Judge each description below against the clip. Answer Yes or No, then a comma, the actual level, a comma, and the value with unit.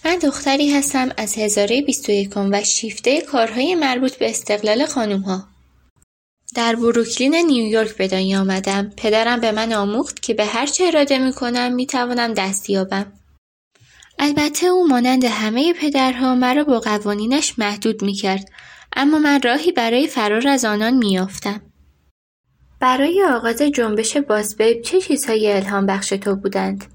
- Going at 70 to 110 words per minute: No, average, 145 wpm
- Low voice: No, high, 230 Hz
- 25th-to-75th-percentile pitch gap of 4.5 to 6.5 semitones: Yes, average, 4.9 semitones